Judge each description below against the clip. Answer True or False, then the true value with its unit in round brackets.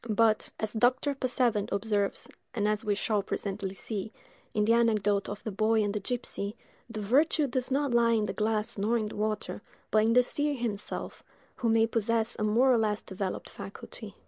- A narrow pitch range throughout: True (2.2 semitones)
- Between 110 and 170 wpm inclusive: False (195 wpm)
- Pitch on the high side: True (220 Hz)